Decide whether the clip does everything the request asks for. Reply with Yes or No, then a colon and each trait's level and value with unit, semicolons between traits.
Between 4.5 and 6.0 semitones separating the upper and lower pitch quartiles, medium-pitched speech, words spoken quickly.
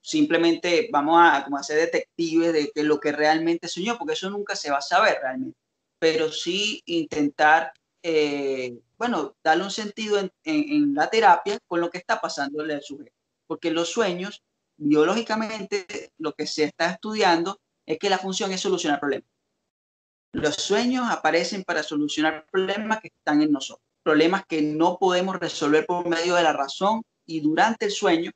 No: average, 5.1 semitones; medium, 170 Hz; average, 170 wpm